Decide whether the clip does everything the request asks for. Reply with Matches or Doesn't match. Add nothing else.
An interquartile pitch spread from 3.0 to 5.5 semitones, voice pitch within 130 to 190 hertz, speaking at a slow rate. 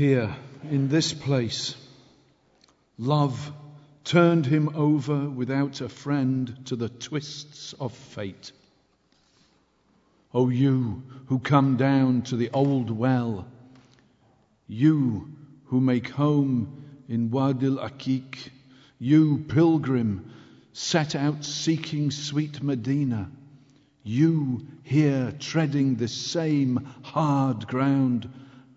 Doesn't match